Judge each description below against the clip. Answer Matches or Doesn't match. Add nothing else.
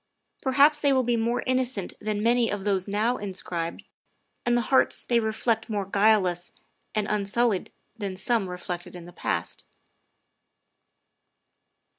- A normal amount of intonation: Matches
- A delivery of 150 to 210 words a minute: Doesn't match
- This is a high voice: Matches